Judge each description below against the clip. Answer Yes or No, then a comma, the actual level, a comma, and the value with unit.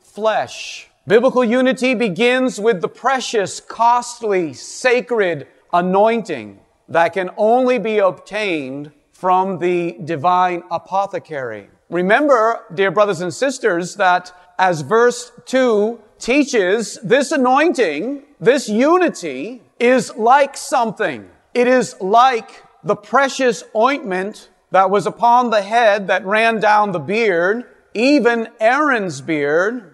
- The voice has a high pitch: Yes, high, 220 Hz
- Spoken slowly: Yes, slow, 110 wpm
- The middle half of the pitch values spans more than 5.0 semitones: Yes, wide, 5.5 semitones